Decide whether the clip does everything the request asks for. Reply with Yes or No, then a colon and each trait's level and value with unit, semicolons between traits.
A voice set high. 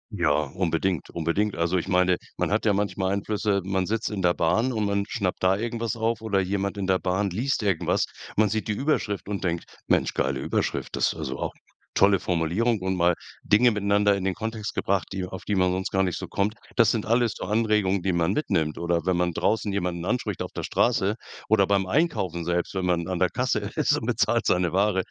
No: very low, 95 Hz